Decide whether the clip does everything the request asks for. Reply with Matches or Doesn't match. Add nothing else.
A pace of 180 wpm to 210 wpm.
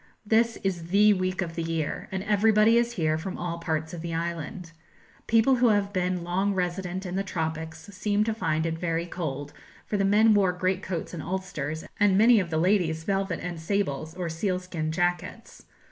Matches